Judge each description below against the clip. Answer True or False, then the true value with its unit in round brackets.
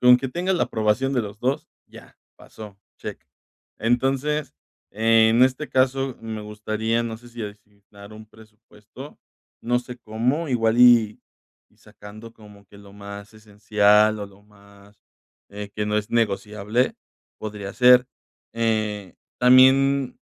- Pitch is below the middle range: True (110 Hz)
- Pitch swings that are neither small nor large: True (3.0 semitones)